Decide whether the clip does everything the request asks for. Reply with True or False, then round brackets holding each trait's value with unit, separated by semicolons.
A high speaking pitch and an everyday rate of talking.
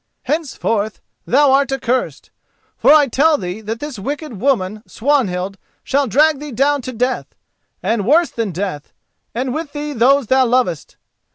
True (260 Hz; 155 wpm)